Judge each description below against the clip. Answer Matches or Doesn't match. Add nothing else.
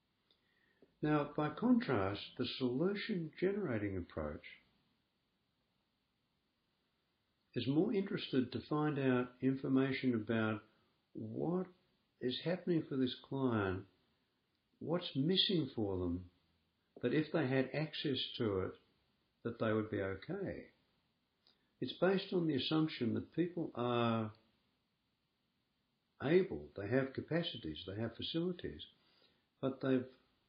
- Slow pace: Matches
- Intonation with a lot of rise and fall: Matches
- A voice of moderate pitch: Doesn't match